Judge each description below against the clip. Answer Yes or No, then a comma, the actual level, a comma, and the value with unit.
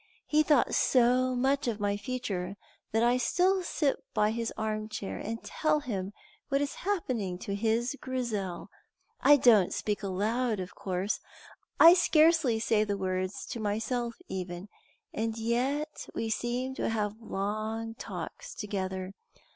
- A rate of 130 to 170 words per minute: Yes, average, 145 wpm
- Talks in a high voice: Yes, high, 225 Hz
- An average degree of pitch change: Yes, average, 4.0 semitones